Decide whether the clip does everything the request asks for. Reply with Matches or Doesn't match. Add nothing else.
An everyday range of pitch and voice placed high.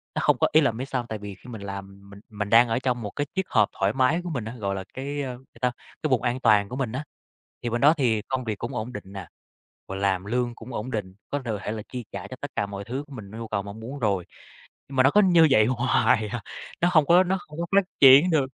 Doesn't match